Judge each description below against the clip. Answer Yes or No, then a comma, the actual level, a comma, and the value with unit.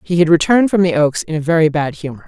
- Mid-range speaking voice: Yes, medium, 165 Hz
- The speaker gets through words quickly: Yes, fast, 290 wpm